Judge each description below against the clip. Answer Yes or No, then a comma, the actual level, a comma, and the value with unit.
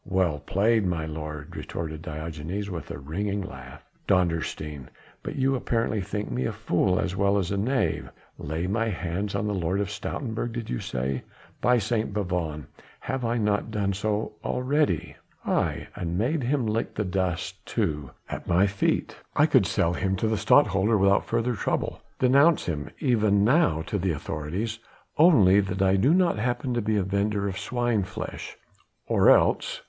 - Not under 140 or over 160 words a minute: No, average, 175 wpm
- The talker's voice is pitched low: Yes, low, 100 Hz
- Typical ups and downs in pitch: Yes, average, 4.8 semitones